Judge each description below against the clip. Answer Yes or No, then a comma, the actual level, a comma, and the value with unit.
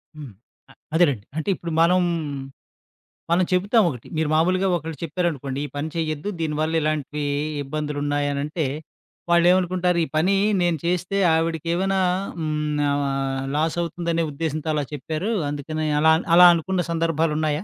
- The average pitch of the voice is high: No, medium, 160 Hz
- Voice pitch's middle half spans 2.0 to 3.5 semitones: Yes, narrow, 2.6 semitones